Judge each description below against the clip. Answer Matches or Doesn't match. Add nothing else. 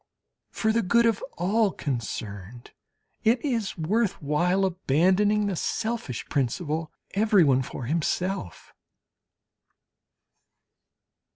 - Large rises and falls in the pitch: Matches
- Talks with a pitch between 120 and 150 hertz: Doesn't match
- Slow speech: Matches